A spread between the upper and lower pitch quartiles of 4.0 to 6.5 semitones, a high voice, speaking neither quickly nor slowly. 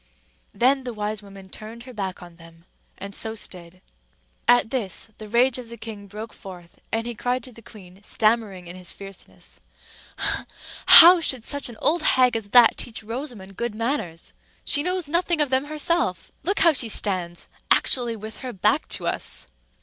Yes: average, 4.6 semitones; high, 225 Hz; average, 175 wpm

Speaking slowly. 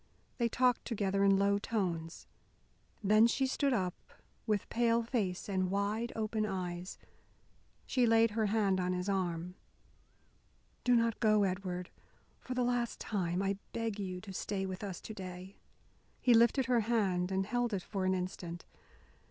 No: average, 160 wpm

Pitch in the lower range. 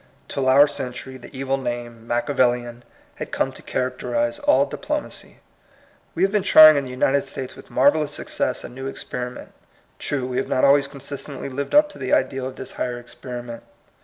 Yes: low, 130 Hz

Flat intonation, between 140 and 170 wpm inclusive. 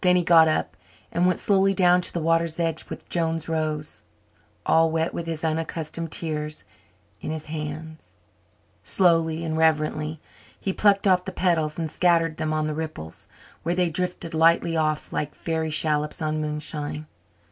Yes: narrow, 1.6 semitones; average, 165 wpm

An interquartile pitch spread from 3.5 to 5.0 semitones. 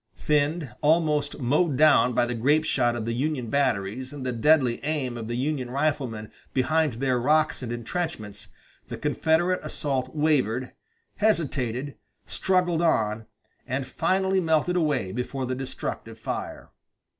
Yes: average, 4.2 semitones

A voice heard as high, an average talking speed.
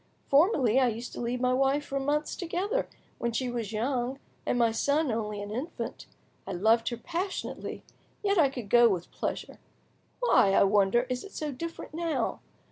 Yes: very high, 250 Hz; average, 180 wpm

